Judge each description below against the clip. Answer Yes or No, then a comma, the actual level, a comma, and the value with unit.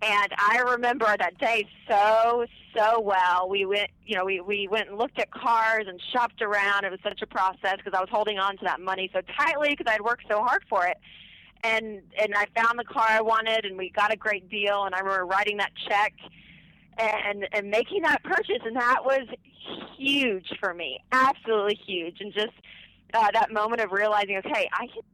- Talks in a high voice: Yes, high, 210 Hz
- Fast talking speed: Yes, fast, 210 wpm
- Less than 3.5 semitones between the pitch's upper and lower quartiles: Yes, narrow, 2.6 semitones